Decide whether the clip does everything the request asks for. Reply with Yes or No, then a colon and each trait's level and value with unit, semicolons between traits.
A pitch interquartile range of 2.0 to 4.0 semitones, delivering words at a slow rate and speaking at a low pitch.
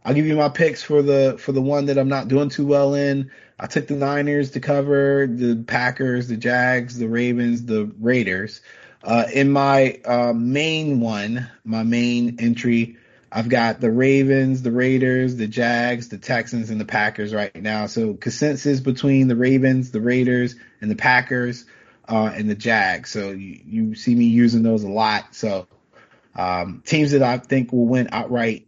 No: average, 2.9 semitones; average, 180 wpm; low, 125 Hz